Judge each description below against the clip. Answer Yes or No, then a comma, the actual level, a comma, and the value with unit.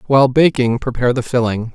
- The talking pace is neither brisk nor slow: Yes, average, 170 wpm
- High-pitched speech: No, low, 125 Hz